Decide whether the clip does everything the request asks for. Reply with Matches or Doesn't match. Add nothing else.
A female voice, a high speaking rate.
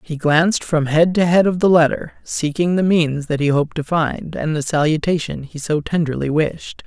Doesn't match